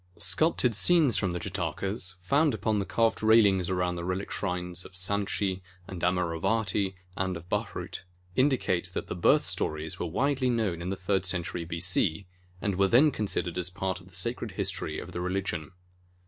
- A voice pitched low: Yes, very low, 95 Hz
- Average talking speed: Yes, average, 175 wpm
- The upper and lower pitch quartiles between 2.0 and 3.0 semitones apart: No, average, 3.4 semitones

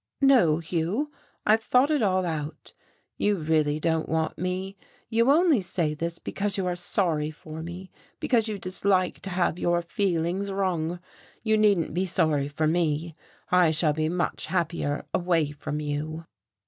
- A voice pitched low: No, medium, 175 Hz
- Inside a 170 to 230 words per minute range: No, average, 160 wpm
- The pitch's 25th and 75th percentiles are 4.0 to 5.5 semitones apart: No, average, 3.6 semitones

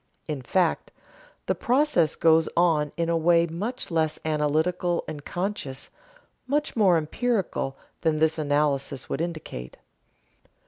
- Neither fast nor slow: No, slow, 125 wpm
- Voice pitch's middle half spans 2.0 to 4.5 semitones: Yes, average, 2.9 semitones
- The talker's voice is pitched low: No, medium, 165 Hz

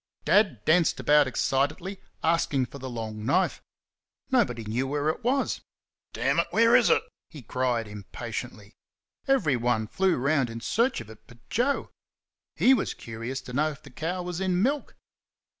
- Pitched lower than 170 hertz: Yes, medium, 140 Hz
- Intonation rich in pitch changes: Yes, wide, 7.7 semitones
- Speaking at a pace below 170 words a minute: Yes, average, 160 wpm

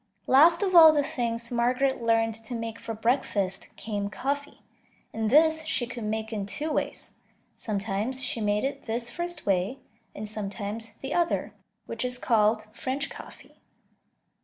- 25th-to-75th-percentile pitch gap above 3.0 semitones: Yes, average, 4.2 semitones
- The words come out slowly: No, average, 155 wpm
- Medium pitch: No, high, 230 Hz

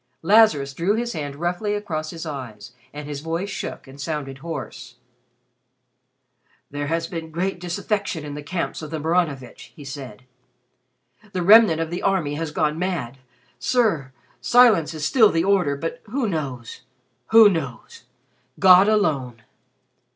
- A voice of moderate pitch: Yes, medium, 165 Hz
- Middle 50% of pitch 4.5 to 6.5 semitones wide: Yes, average, 5.1 semitones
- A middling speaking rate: Yes, average, 145 wpm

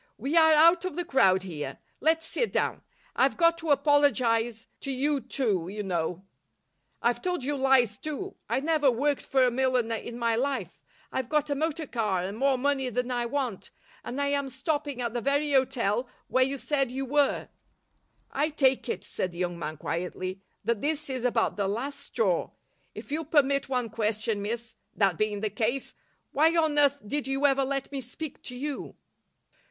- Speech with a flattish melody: No, average, 4.2 semitones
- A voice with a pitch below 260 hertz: No, very high, 265 Hz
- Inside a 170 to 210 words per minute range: Yes, average, 190 wpm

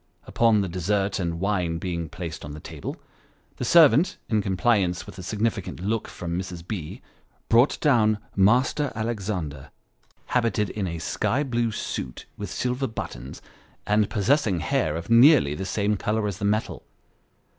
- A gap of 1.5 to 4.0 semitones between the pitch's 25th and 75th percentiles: No, average, 4.7 semitones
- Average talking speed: Yes, average, 155 wpm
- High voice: No, low, 100 Hz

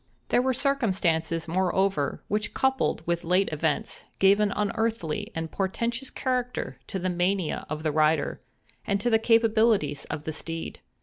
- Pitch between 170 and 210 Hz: Yes, high, 190 Hz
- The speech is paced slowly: No, average, 150 wpm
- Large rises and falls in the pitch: Yes, wide, 5.8 semitones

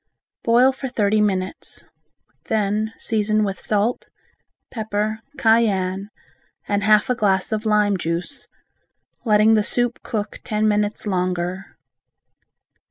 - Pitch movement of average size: No, narrow, 1.8 semitones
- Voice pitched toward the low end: No, high, 210 Hz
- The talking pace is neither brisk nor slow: No, slow, 110 wpm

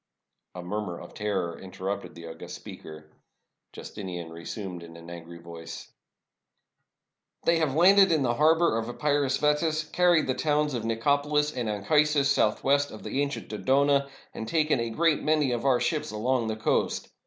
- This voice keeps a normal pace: Yes, average, 160 wpm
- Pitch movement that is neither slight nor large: No, wide, 7.1 semitones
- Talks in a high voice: No, low, 130 Hz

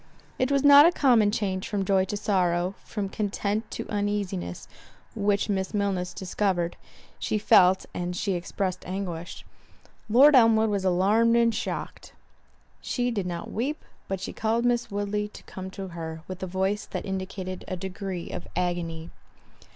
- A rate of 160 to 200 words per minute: No, average, 150 wpm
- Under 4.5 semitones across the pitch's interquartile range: Yes, average, 2.8 semitones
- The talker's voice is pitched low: No, high, 195 Hz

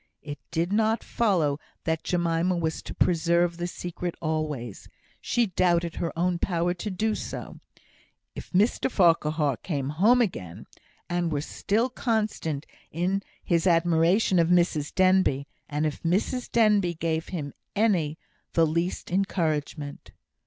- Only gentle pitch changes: No, average, 3.0 semitones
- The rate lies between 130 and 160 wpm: Yes, slow, 135 wpm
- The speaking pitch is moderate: Yes, medium, 170 Hz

